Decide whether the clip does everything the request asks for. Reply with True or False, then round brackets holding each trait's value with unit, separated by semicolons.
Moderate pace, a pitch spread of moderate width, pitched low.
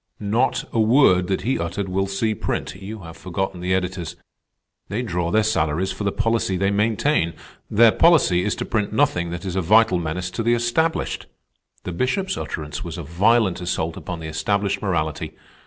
True (185 wpm; 4.1 semitones; 95 Hz)